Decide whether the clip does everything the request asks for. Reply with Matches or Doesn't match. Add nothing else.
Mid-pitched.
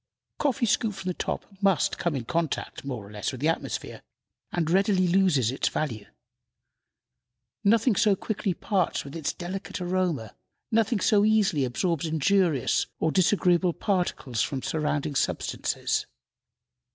Matches